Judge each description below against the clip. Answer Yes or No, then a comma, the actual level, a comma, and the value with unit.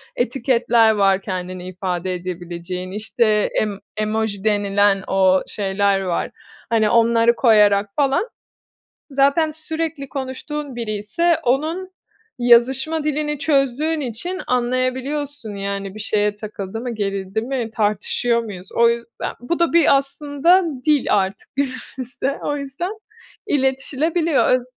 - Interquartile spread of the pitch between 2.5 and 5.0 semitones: No, wide, 5.6 semitones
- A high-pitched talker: Yes, high, 235 Hz